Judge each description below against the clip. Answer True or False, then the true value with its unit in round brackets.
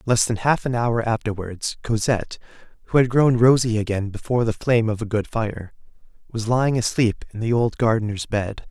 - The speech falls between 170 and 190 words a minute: True (185 wpm)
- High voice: False (115 Hz)